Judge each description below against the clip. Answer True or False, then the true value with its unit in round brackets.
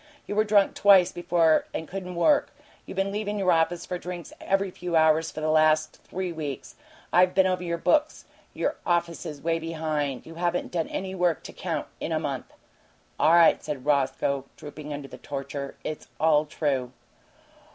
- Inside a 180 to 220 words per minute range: True (185 wpm)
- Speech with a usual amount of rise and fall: True (3.1 semitones)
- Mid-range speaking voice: True (165 Hz)